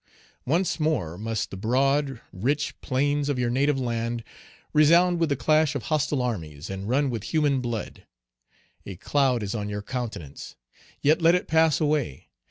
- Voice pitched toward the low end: Yes, low, 130 Hz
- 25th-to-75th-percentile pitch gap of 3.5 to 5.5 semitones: Yes, average, 5.1 semitones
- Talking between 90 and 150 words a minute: No, average, 165 wpm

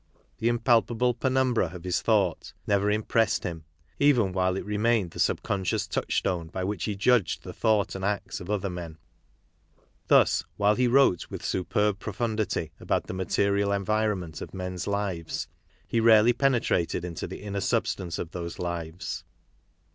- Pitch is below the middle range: Yes, low, 100 Hz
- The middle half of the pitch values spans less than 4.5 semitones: Yes, average, 3.6 semitones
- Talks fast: No, average, 160 wpm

